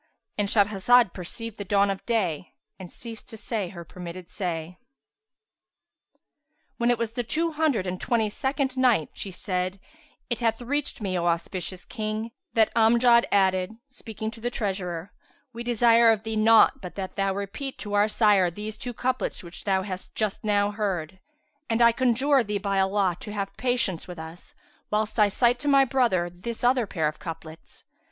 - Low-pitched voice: No, high, 210 Hz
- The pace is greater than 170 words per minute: Yes, average, 180 wpm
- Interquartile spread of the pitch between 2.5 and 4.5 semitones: Yes, average, 4.0 semitones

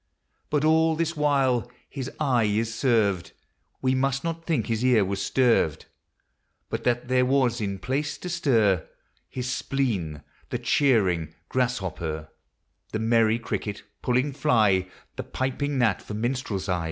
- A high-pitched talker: No, low, 120 Hz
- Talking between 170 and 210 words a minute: No, average, 140 wpm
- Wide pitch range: No, average, 4.8 semitones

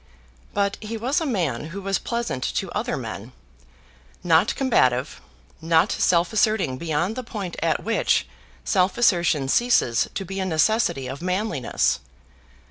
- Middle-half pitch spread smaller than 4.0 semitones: No, average, 5.3 semitones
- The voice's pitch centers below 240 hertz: Yes, medium, 185 Hz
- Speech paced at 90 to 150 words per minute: Yes, average, 140 wpm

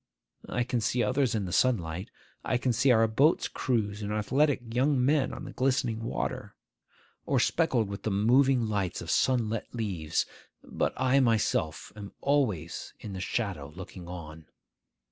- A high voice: No, low, 115 Hz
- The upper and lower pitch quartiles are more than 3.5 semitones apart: Yes, average, 4.6 semitones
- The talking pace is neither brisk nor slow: Yes, average, 165 wpm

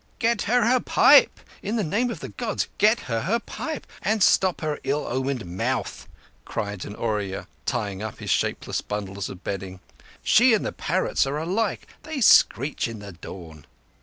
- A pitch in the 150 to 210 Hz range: No, medium, 140 Hz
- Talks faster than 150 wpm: Yes, average, 175 wpm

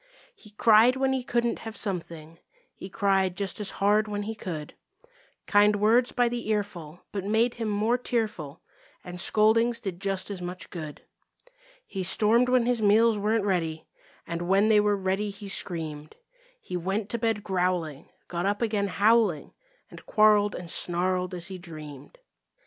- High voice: Yes, high, 205 Hz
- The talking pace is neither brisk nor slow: Yes, average, 165 wpm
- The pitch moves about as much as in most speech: Yes, average, 3.6 semitones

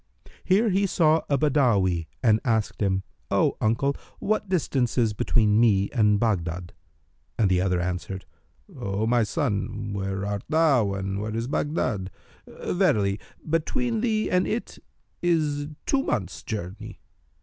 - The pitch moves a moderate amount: No, wide, 7.7 semitones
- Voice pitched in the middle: No, low, 110 Hz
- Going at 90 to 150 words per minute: Yes, average, 140 wpm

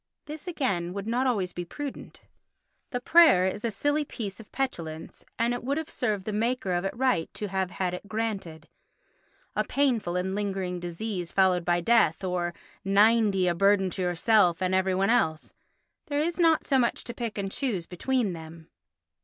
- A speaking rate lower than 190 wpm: Yes, average, 180 wpm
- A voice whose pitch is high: Yes, high, 200 Hz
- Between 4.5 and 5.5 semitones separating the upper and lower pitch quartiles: Yes, average, 5.2 semitones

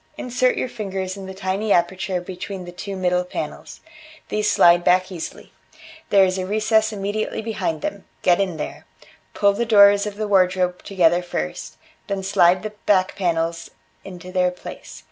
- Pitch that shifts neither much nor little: No, narrow, 2.3 semitones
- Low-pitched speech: No, high, 190 Hz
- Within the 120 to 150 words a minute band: No, average, 165 wpm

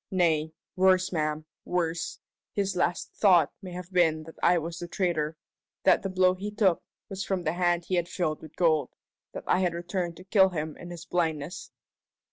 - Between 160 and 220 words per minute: Yes, average, 190 wpm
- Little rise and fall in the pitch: Yes, narrow, 2.3 semitones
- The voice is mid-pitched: Yes, medium, 175 Hz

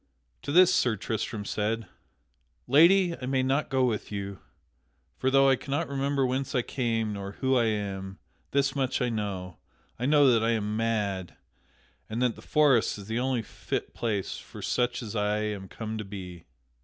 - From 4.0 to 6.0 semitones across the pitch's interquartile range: Yes, average, 4.3 semitones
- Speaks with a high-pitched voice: No, low, 115 Hz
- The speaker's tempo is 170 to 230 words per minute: Yes, average, 180 wpm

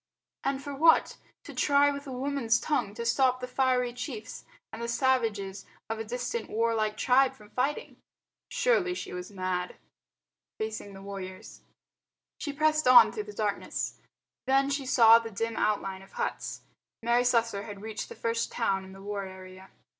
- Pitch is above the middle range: Yes, high, 230 Hz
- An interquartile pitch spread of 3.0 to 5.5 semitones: Yes, average, 4.9 semitones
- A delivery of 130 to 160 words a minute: No, average, 170 wpm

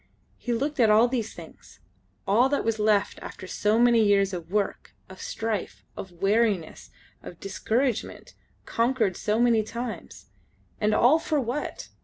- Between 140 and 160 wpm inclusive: Yes, average, 150 wpm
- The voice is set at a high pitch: Yes, high, 220 Hz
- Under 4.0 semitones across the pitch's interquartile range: Yes, average, 3.2 semitones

